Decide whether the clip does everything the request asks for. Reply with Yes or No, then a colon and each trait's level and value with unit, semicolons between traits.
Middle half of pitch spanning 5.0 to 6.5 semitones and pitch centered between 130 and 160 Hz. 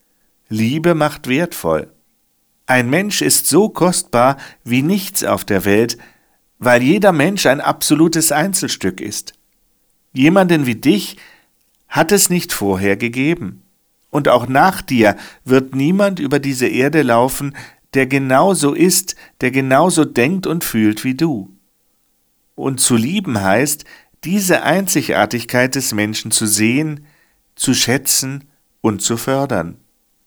Yes: average, 5.3 semitones; low, 135 Hz